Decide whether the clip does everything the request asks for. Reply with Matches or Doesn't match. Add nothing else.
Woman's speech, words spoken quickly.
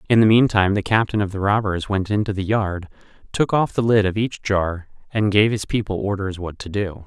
Doesn't match